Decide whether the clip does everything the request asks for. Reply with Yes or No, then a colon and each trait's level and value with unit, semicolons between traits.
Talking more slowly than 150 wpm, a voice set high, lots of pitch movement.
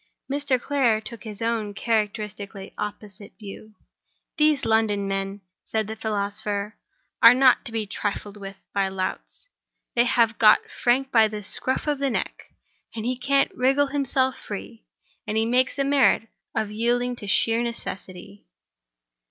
No: average, 140 wpm; high, 220 Hz; average, 3.5 semitones